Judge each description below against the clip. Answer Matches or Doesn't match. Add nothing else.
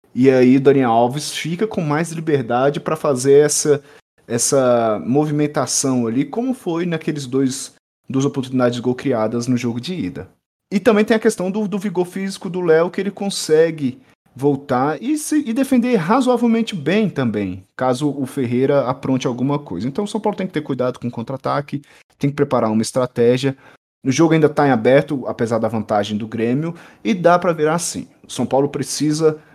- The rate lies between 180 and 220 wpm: Matches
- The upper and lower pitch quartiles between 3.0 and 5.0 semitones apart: Doesn't match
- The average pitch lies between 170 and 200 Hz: Doesn't match